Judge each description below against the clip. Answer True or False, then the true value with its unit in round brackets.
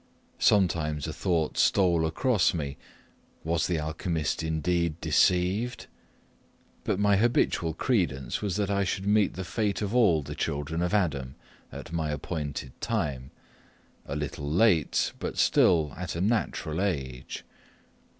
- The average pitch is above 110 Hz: False (85 Hz)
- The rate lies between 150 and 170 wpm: False (135 wpm)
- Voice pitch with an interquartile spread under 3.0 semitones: False (4.7 semitones)